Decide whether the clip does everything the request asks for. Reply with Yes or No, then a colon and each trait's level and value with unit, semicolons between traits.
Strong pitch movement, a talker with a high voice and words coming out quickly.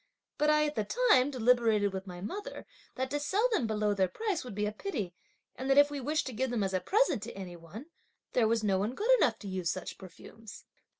Yes: wide, 6.4 semitones; high, 230 Hz; fast, 240 wpm